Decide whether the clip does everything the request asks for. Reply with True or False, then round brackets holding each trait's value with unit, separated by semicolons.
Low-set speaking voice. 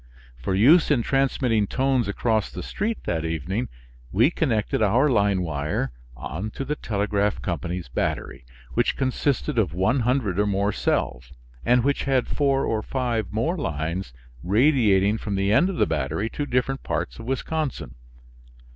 True (110 Hz)